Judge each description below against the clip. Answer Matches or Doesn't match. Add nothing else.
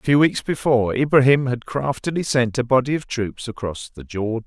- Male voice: Matches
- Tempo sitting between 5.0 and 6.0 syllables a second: Matches